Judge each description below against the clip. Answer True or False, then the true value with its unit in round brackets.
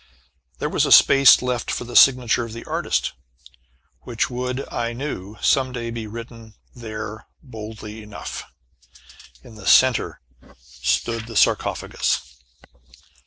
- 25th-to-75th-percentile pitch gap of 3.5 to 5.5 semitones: False (2.5 semitones)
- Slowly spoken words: True (125 wpm)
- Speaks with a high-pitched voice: False (115 Hz)